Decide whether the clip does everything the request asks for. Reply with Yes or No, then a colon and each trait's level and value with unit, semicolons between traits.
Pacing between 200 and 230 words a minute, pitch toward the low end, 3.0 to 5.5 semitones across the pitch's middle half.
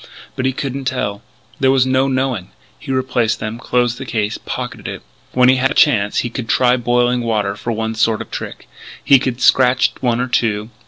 No: fast, 205 wpm; low, 125 Hz; narrow, 2.5 semitones